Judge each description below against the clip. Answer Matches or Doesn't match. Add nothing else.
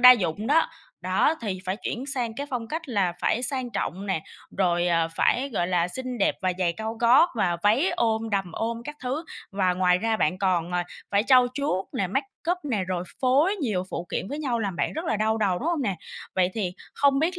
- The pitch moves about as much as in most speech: Doesn't match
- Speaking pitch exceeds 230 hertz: Doesn't match